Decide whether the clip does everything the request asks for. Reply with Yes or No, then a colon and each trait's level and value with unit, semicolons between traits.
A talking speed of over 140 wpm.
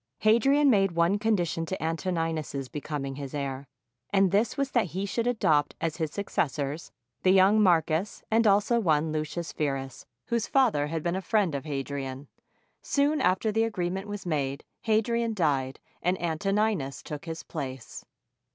Yes: average, 160 wpm